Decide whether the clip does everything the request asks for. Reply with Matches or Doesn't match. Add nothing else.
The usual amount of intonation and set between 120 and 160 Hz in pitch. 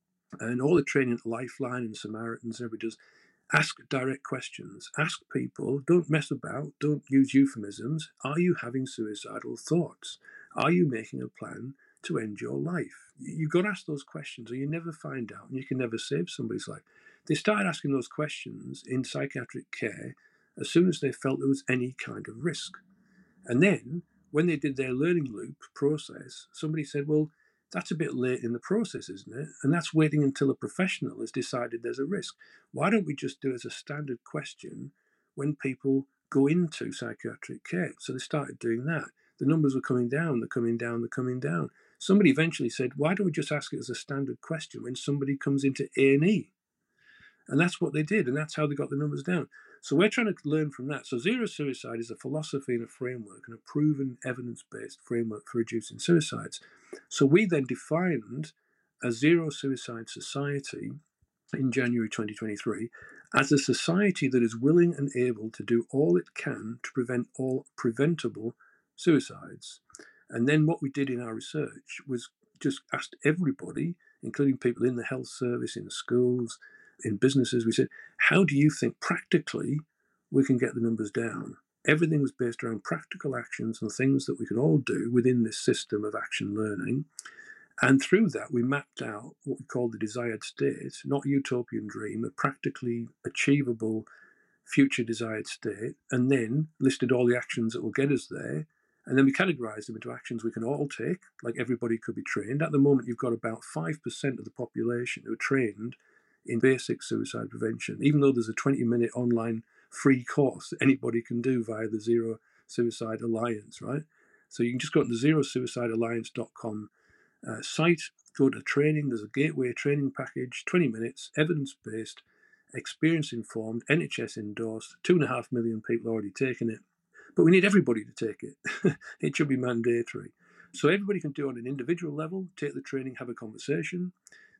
Matches